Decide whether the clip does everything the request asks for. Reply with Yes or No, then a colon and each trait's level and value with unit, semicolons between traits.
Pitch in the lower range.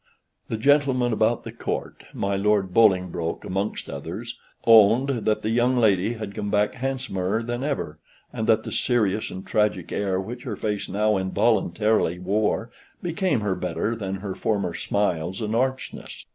Yes: low, 105 Hz